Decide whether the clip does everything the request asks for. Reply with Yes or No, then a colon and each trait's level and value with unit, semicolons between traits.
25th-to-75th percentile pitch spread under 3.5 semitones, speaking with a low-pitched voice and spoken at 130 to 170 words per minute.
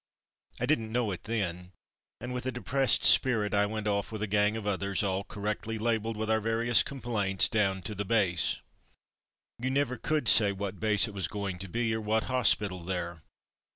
No: narrow, 2.6 semitones; low, 105 Hz; average, 190 wpm